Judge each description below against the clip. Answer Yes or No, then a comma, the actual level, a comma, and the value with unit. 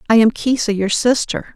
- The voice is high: Yes, high, 225 Hz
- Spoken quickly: No, average, 195 wpm